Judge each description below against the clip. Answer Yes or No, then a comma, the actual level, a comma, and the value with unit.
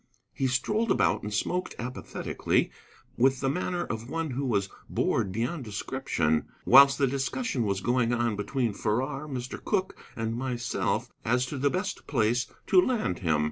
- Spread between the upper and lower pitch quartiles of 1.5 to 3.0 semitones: No, average, 3.8 semitones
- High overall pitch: No, low, 125 Hz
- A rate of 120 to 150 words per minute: No, average, 160 wpm